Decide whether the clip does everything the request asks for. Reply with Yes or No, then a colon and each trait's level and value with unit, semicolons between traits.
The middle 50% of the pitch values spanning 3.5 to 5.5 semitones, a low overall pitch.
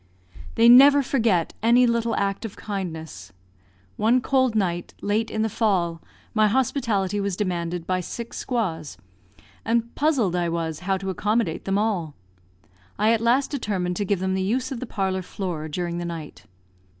No: average, 4.7 semitones; high, 200 Hz